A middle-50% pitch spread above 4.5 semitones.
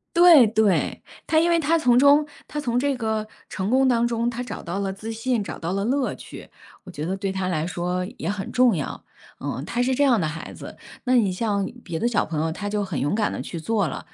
Yes: average, 5.0 semitones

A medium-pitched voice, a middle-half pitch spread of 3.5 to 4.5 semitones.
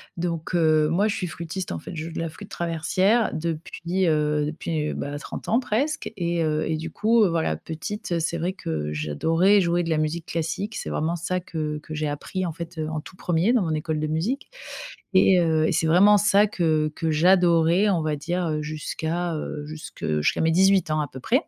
No: medium, 165 Hz; average, 2.8 semitones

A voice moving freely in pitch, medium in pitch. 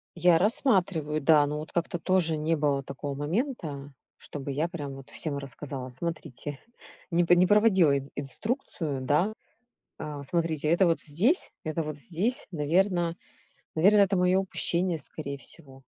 No: average, 3.9 semitones; medium, 160 Hz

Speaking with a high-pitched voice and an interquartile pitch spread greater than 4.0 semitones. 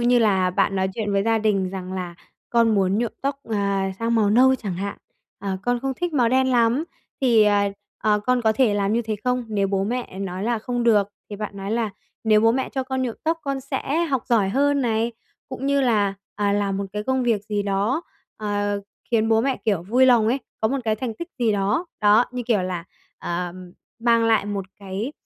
No: high, 220 Hz; average, 3.6 semitones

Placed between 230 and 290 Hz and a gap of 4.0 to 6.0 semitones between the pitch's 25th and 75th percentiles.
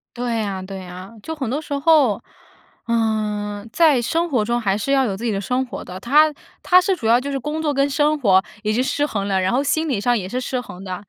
Yes: high, 240 Hz; wide, 5.6 semitones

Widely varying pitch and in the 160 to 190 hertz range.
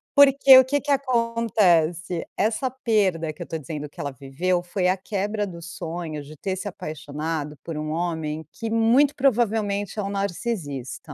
Yes: wide, 6.1 semitones; medium, 185 Hz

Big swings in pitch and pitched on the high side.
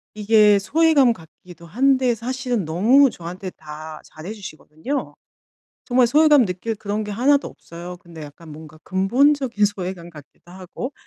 Yes: wide, 6.8 semitones; high, 205 Hz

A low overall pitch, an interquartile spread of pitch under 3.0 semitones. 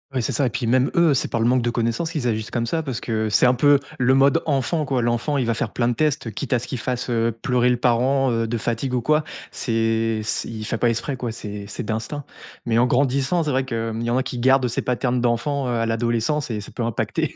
Yes: low, 120 Hz; narrow, 2.6 semitones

